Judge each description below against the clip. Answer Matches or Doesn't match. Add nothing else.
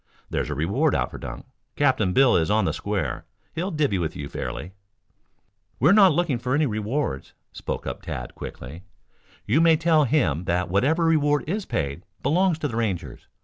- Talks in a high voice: Doesn't match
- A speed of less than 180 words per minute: Doesn't match